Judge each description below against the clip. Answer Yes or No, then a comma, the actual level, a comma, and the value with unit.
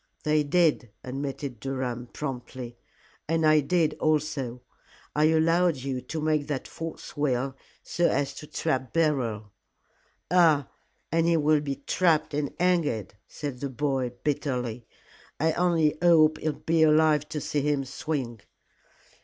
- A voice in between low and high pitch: Yes, medium, 150 Hz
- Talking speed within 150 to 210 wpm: No, slow, 135 wpm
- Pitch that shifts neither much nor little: Yes, average, 3.2 semitones